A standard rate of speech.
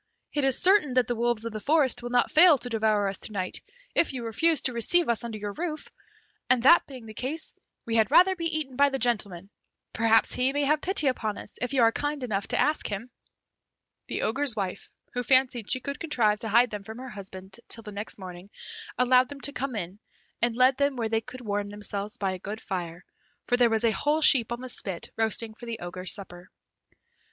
No: fast, 225 wpm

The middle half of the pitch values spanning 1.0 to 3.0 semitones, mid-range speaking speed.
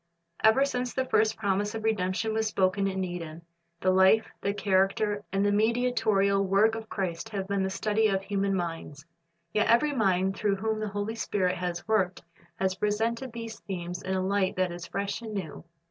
Yes: average, 2.7 semitones; average, 190 wpm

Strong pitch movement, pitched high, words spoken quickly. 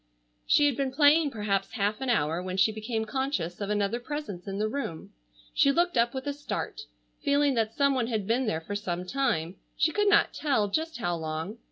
Yes: wide, 6.1 semitones; high, 230 Hz; fast, 210 wpm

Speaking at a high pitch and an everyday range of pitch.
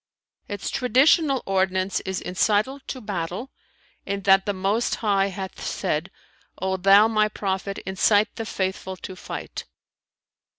No: high, 195 Hz; narrow, 2.2 semitones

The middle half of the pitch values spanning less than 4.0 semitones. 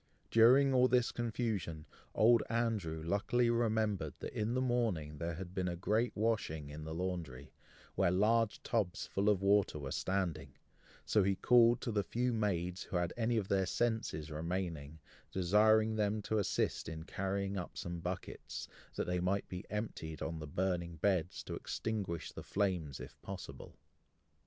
No: average, 4.7 semitones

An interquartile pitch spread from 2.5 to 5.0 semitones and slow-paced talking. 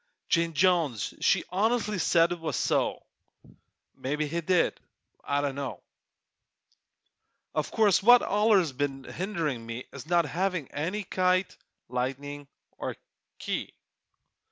Yes: average, 4.7 semitones; slow, 115 wpm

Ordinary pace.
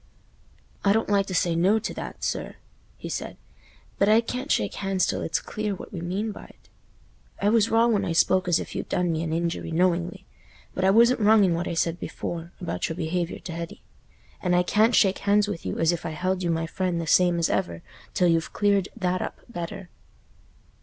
No: fast, 215 wpm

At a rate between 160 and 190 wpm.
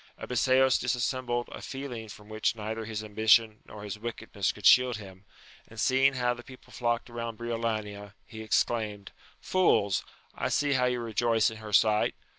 Yes: average, 170 wpm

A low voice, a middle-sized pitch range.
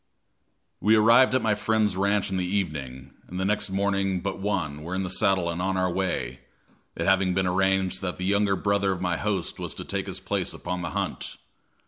No: very low, 95 Hz; narrow, 1.9 semitones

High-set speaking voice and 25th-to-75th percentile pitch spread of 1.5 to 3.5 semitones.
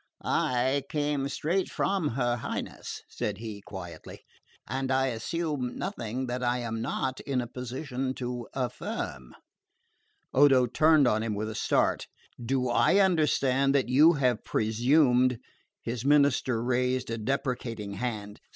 No: low, 125 Hz; average, 3.0 semitones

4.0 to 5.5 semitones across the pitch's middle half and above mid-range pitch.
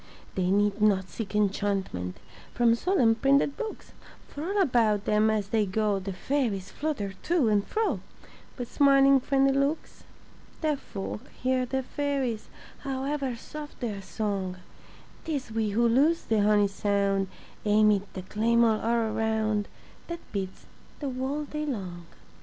Yes: average, 5.2 semitones; high, 225 Hz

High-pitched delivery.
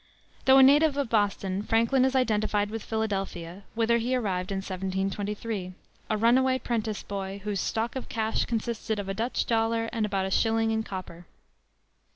Yes: high, 220 Hz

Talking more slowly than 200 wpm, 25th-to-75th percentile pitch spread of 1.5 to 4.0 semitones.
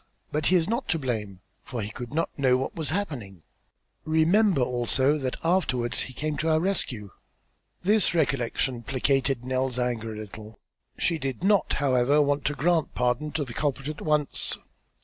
No: average, 170 wpm; average, 4.4 semitones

